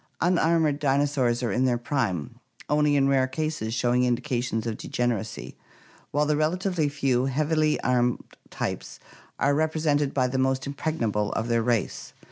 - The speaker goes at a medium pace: Yes, average, 145 wpm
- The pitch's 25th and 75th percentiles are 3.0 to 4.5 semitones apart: Yes, average, 3.6 semitones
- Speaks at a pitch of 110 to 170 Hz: Yes, low, 135 Hz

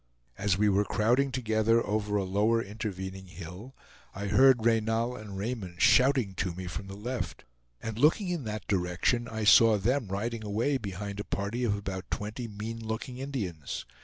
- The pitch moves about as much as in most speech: Yes, average, 3.2 semitones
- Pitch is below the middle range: Yes, low, 105 Hz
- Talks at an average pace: Yes, average, 170 wpm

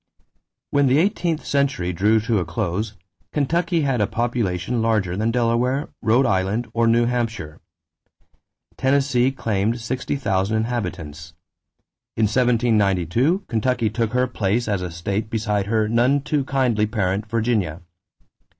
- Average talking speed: No, slow, 130 wpm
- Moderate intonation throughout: Yes, average, 3.8 semitones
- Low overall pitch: Yes, low, 115 Hz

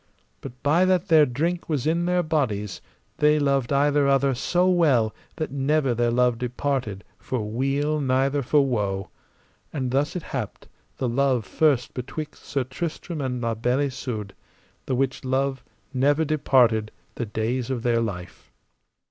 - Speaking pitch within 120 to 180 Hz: Yes, low, 135 Hz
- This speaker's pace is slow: No, average, 155 wpm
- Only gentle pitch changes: No, average, 3.5 semitones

